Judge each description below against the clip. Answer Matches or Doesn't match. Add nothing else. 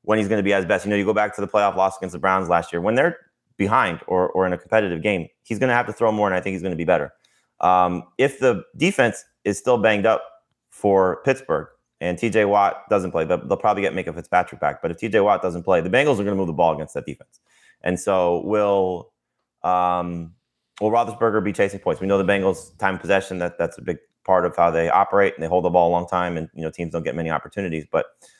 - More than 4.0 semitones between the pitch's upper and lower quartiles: Doesn't match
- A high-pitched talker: Doesn't match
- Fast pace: Matches